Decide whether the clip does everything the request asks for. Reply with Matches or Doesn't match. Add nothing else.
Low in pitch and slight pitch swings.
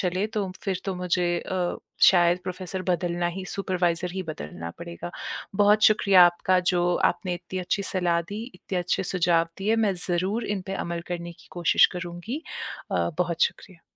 Doesn't match